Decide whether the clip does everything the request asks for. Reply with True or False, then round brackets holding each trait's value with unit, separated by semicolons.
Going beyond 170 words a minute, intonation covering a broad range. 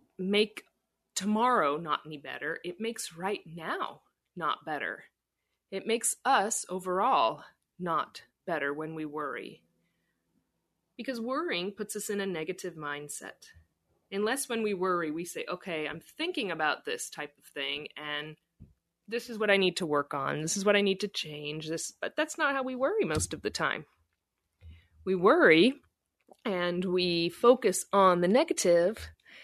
False (155 wpm; 5.7 semitones)